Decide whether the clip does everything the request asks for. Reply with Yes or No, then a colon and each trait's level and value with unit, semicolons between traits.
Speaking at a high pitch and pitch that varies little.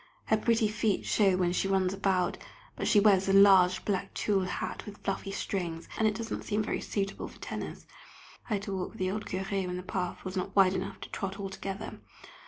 Yes: high, 195 Hz; narrow, 1.8 semitones